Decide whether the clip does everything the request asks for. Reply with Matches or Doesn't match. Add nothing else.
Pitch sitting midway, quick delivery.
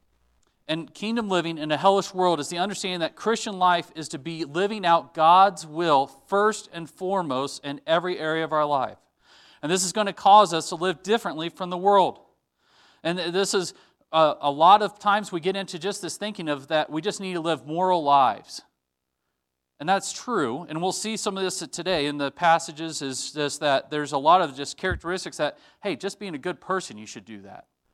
Matches